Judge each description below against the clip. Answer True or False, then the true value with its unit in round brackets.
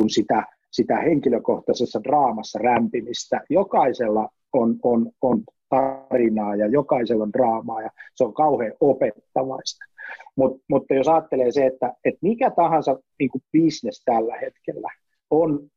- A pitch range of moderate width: True (4.1 semitones)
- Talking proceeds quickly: False (125 wpm)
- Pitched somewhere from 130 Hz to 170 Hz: True (135 Hz)